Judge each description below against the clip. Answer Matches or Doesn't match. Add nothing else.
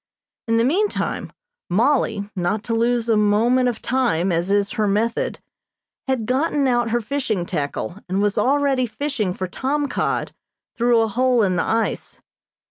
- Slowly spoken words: Doesn't match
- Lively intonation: Doesn't match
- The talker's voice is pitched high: Matches